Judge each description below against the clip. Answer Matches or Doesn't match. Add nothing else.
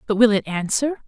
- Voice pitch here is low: Doesn't match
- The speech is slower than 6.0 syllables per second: Matches